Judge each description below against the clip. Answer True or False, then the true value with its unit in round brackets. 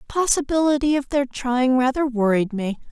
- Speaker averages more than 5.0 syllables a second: True (5.6 syllables/s)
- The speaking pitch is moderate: False (260 Hz)